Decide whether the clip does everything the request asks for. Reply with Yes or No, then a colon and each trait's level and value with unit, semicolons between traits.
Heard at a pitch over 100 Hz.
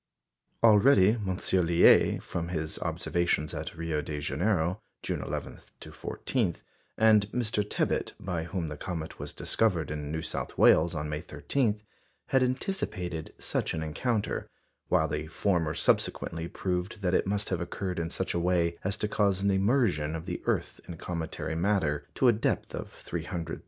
No: very low, 90 Hz